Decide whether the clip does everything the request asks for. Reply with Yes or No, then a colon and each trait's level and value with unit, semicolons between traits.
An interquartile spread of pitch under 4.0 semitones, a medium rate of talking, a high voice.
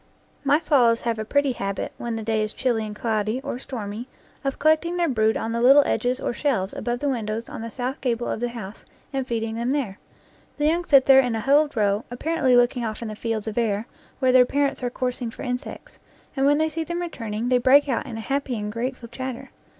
No: average, 3.5 semitones; fast, 235 wpm; high, 245 Hz